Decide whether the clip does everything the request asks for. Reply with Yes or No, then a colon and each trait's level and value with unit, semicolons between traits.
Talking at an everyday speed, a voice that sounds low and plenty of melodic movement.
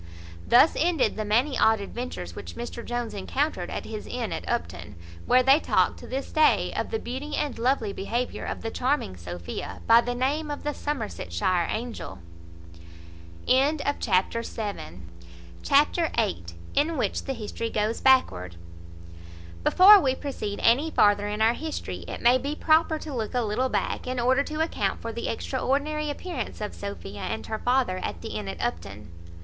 No: average, 165 wpm; high, 240 Hz; wide, 5.7 semitones